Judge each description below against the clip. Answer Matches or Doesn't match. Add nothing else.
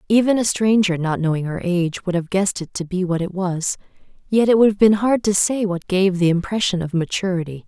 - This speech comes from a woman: Matches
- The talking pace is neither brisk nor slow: Doesn't match